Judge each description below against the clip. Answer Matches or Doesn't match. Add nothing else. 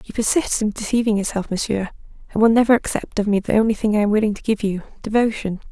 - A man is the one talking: Doesn't match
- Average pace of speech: Doesn't match